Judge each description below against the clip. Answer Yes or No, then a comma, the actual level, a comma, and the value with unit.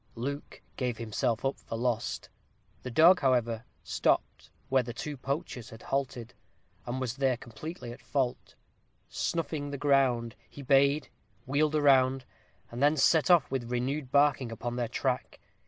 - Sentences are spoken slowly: No, average, 150 wpm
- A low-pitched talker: Yes, low, 130 Hz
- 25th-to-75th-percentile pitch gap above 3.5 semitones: No, average, 2.8 semitones